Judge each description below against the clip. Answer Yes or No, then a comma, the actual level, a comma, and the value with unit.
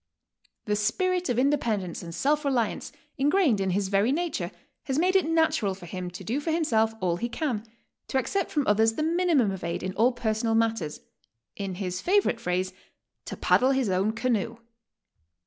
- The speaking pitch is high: Yes, high, 225 Hz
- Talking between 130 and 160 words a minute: No, average, 185 wpm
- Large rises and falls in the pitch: Yes, wide, 7.1 semitones